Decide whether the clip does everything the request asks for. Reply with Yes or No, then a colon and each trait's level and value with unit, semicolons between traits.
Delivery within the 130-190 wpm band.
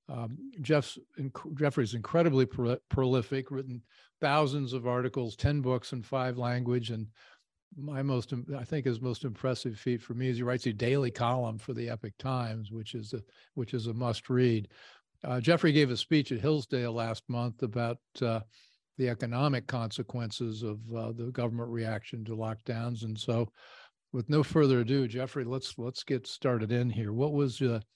Yes: average, 175 wpm